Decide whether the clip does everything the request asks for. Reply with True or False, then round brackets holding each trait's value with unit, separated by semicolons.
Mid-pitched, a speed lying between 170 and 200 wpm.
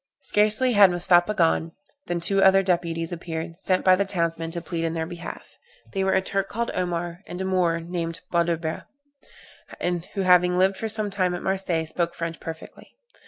True (175 Hz; 180 wpm)